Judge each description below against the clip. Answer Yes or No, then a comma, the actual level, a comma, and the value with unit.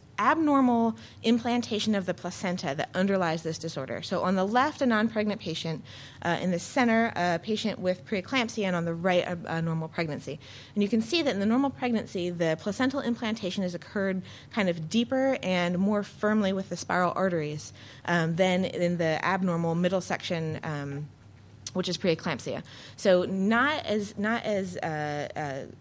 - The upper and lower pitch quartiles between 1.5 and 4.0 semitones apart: No, average, 4.5 semitones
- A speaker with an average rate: Yes, average, 175 wpm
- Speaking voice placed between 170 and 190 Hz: Yes, medium, 185 Hz